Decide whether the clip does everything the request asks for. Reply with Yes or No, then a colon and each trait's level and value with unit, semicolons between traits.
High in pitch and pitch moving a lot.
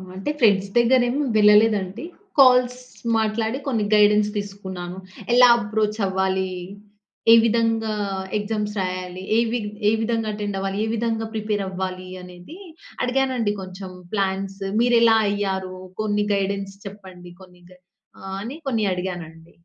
No: high, 205 Hz; average, 2.9 semitones